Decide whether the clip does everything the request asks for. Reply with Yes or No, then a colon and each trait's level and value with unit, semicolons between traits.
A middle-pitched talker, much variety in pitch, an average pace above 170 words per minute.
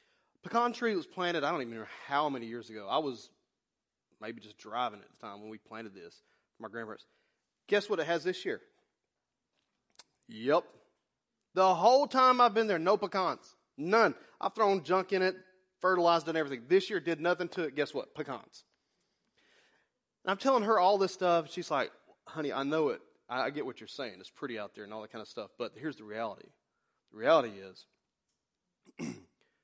Yes: medium, 180 Hz; wide, 6.3 semitones; average, 195 wpm